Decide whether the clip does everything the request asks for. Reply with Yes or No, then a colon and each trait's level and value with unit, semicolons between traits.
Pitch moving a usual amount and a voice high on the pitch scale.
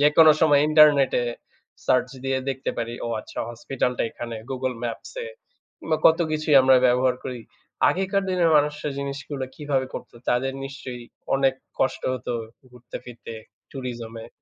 No: average, 3.2 semitones; low, 135 Hz